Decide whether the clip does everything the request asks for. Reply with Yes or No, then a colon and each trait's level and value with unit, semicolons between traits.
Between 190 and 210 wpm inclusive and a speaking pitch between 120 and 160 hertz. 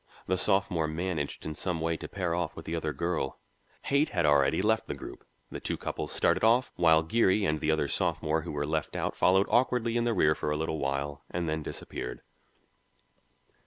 No: average, 200 wpm; very low, 80 Hz